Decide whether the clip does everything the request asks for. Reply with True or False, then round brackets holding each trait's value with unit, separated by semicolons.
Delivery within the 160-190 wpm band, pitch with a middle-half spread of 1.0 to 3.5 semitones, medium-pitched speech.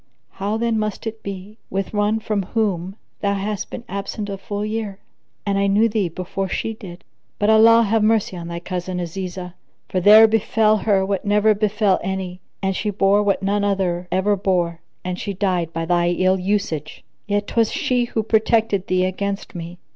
False (185 wpm; 2.6 semitones; 200 Hz)